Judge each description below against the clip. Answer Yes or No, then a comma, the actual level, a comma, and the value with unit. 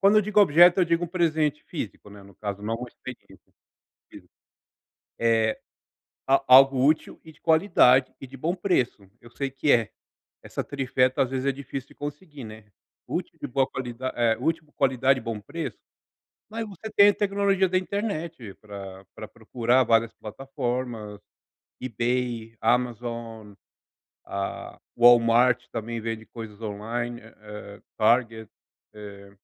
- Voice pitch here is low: Yes, low, 125 Hz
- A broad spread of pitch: No, average, 4.7 semitones